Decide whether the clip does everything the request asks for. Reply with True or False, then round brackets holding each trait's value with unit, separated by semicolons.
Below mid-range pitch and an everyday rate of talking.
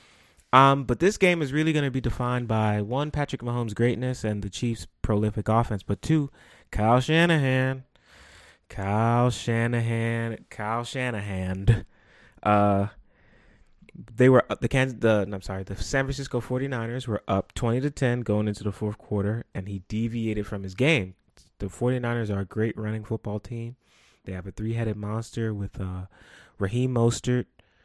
True (115 Hz; 160 wpm)